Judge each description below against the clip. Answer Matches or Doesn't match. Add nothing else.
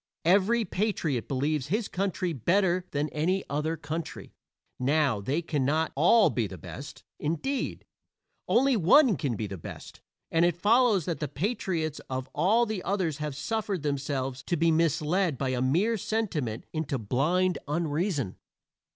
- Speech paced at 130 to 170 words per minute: Matches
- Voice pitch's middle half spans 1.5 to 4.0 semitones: Doesn't match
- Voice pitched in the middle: Matches